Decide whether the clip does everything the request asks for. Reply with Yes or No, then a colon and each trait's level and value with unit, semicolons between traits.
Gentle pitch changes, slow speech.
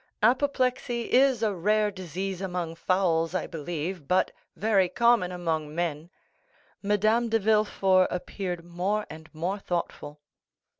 No: average, 3.8 semitones; slow, 120 wpm